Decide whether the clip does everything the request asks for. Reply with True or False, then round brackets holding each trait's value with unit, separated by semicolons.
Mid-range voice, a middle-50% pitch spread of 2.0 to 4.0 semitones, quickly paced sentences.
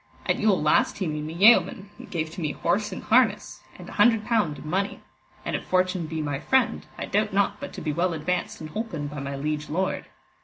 False (180 Hz; 5.3 semitones; 230 wpm)